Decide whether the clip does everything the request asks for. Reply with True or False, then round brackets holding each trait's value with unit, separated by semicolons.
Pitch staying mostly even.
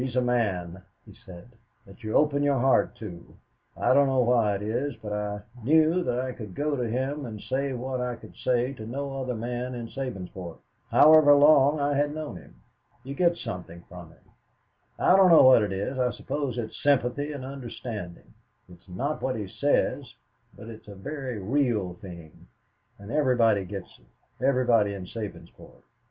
False (5.1 semitones)